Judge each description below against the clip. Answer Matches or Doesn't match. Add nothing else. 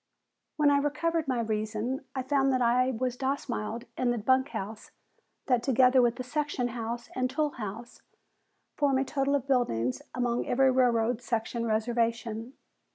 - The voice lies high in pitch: Matches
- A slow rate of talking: Doesn't match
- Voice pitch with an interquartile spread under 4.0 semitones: Matches